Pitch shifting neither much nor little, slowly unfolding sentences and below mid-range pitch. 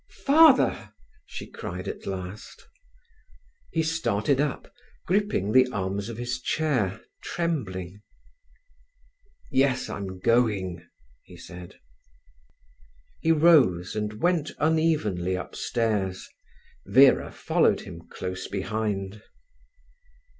No: wide, 7.9 semitones; slow, 90 wpm; low, 110 Hz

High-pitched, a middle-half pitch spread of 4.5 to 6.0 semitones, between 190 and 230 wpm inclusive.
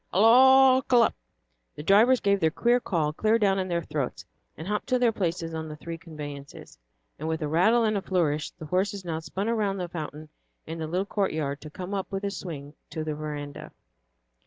No: medium, 175 Hz; average, 4.9 semitones; fast, 205 wpm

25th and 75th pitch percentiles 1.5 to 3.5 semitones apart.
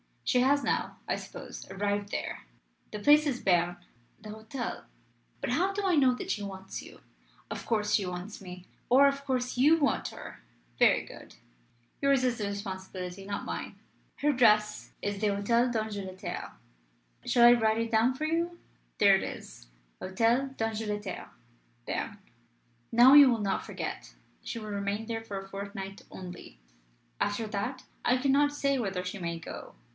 No: average, 4.3 semitones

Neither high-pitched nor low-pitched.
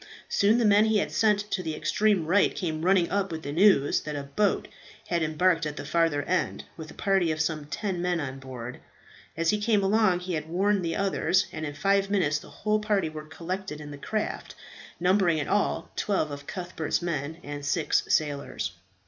Yes: medium, 170 Hz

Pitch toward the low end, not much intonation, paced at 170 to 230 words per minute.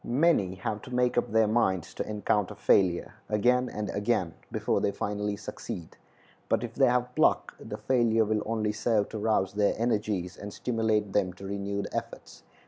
Yes: low, 105 Hz; narrow, 2.3 semitones; average, 175 wpm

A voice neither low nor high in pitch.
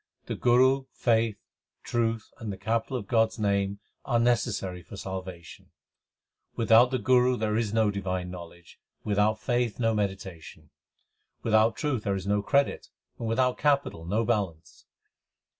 No: low, 110 Hz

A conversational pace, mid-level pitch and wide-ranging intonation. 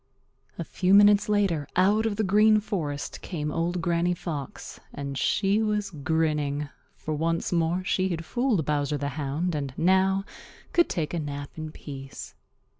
No: average, 160 wpm; medium, 170 Hz; average, 4.7 semitones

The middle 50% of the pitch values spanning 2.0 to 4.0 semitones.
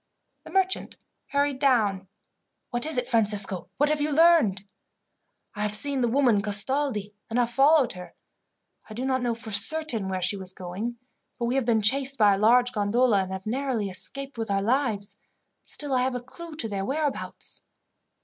No: average, 5.1 semitones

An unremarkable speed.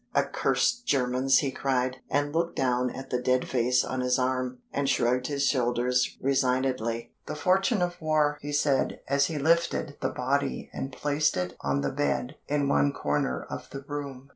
Yes: average, 175 wpm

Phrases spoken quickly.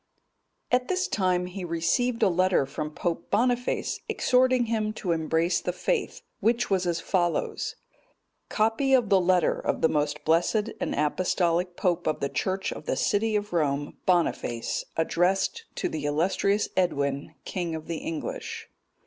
No: average, 155 wpm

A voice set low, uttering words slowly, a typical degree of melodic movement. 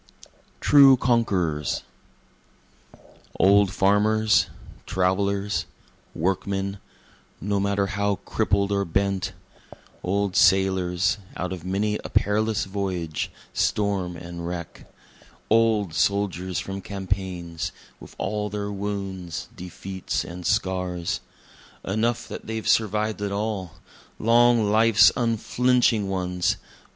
No: low, 100 Hz; slow, 100 wpm; narrow, 2.3 semitones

